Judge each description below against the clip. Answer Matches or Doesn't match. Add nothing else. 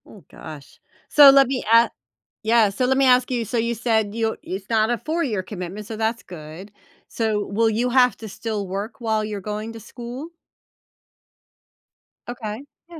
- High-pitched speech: Matches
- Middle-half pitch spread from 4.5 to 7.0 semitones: Doesn't match